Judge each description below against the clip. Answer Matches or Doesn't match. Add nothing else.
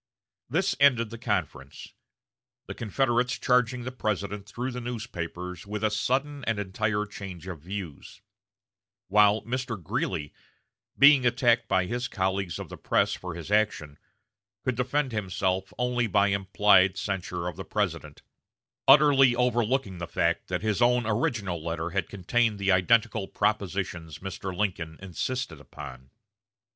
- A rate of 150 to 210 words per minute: Doesn't match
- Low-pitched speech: Matches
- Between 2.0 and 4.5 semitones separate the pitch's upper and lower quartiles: Doesn't match